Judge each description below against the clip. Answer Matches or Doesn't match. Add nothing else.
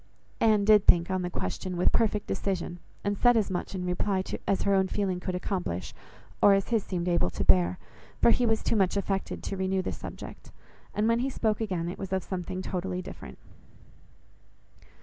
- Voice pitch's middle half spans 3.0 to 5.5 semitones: Doesn't match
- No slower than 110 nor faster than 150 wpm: Doesn't match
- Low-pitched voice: Doesn't match